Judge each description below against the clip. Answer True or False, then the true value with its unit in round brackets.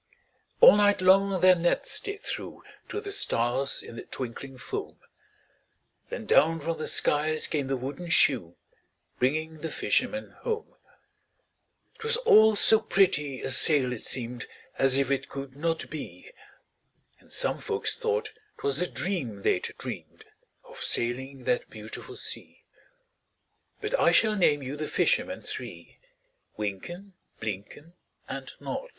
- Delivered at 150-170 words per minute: False (140 wpm)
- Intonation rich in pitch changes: True (7.3 semitones)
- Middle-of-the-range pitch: True (155 Hz)